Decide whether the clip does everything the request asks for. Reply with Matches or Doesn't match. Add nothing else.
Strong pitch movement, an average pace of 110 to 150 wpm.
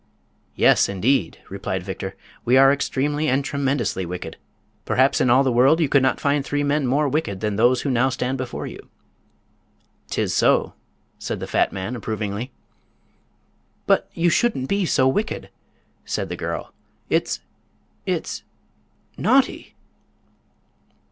Doesn't match